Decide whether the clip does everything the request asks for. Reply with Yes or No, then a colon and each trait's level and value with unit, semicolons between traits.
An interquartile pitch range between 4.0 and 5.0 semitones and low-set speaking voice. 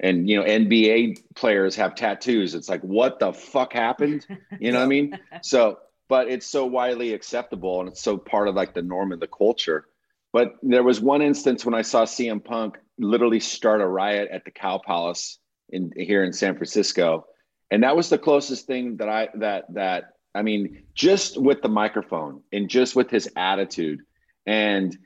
Yes: average, 4.4 semitones; low, 115 Hz